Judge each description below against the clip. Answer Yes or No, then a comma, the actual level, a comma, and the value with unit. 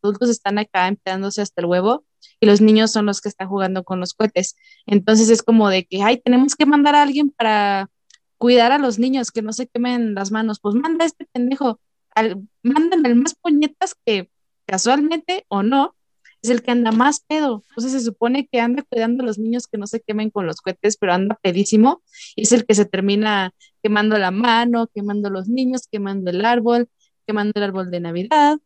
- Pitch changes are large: No, average, 3.8 semitones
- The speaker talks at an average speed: No, fast, 205 wpm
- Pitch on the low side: No, high, 225 Hz